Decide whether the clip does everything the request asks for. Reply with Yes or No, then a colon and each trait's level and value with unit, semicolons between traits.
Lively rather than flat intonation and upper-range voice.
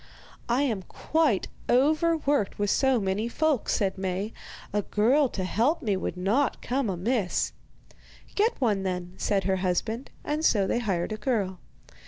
Yes: wide, 5.9 semitones; high, 215 Hz